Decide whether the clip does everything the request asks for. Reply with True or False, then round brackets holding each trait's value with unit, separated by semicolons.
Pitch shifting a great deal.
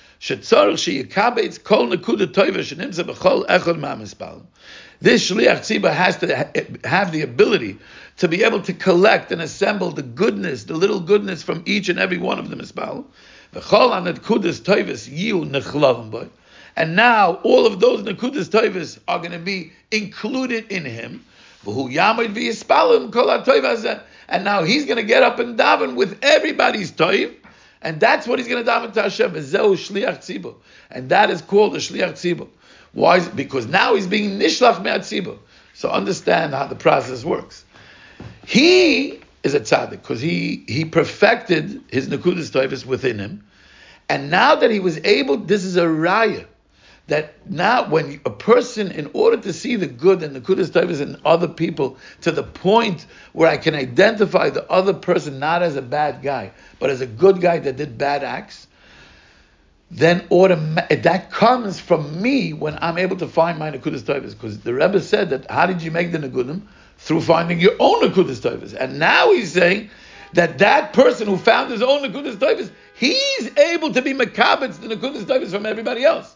True (6.2 semitones)